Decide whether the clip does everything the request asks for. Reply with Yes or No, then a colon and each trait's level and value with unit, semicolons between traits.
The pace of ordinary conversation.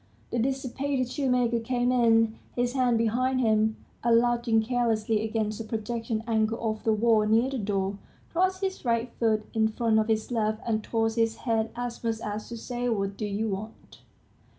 Yes: average, 180 wpm